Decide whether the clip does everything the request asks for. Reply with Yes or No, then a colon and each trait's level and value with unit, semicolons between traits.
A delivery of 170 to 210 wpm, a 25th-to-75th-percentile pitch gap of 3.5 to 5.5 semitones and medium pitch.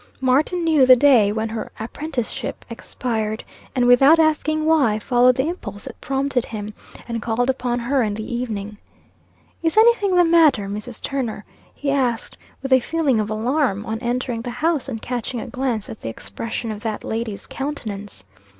No: average, 175 wpm; average, 4.2 semitones; high, 245 Hz